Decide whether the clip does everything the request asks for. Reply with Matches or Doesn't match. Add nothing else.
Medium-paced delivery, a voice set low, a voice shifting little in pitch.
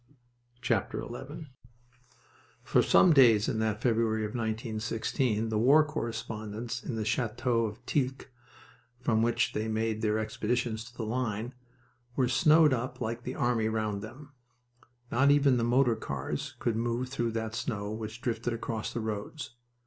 Matches